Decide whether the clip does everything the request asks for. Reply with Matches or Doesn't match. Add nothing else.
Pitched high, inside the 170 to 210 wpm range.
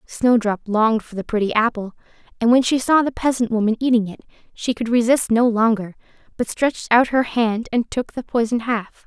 Matches